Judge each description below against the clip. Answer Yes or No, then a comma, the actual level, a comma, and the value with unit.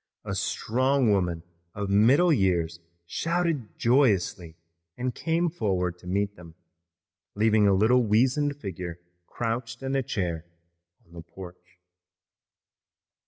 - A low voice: Yes, low, 105 Hz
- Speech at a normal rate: No, slow, 120 wpm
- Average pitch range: No, wide, 6.3 semitones